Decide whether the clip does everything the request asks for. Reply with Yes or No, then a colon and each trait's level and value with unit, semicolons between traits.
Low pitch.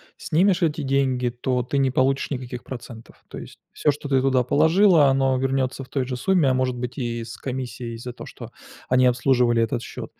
Yes: low, 130 Hz